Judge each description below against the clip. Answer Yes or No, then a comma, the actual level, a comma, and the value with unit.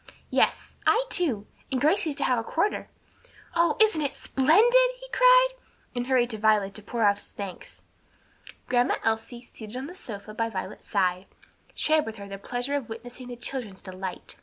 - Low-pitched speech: No, high, 245 Hz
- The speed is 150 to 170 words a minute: No, average, 180 wpm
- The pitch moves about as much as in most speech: No, wide, 6.3 semitones